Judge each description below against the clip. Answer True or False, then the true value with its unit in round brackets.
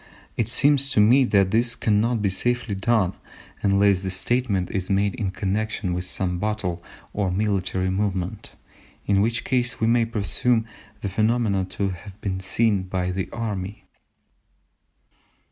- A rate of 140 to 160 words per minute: True (145 wpm)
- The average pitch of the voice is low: True (100 Hz)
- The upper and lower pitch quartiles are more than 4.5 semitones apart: False (3.4 semitones)